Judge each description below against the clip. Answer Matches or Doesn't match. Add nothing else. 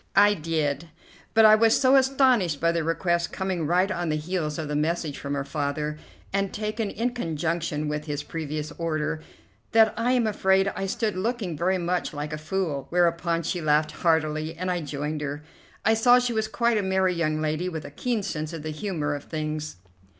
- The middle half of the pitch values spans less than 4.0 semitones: Doesn't match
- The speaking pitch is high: Doesn't match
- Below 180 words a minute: Doesn't match